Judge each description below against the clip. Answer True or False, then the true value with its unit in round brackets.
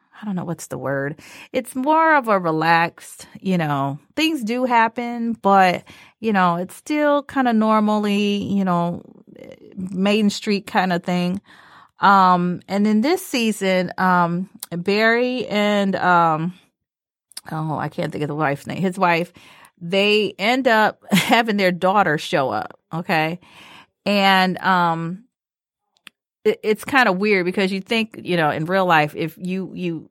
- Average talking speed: True (155 wpm)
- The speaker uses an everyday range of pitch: True (3.9 semitones)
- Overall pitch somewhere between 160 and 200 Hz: True (190 Hz)